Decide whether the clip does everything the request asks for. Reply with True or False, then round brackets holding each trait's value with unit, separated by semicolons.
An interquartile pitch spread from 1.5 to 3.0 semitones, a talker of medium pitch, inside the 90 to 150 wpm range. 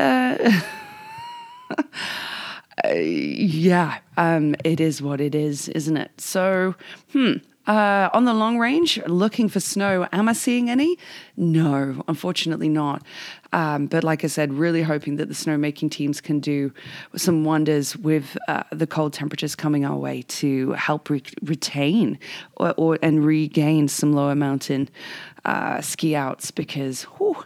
False (5.3 semitones; 160 Hz; 145 wpm)